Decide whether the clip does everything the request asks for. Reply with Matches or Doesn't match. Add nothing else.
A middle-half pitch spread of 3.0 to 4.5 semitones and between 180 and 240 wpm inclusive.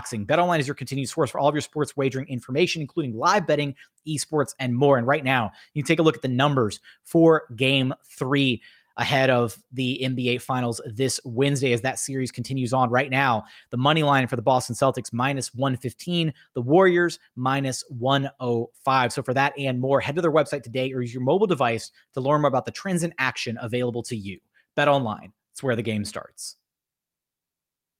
Doesn't match